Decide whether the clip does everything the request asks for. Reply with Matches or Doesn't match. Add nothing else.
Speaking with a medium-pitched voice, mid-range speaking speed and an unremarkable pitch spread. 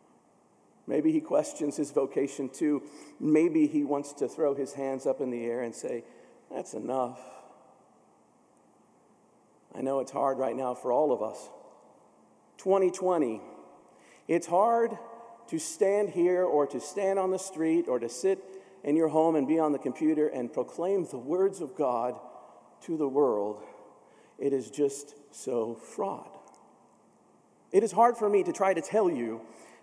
Doesn't match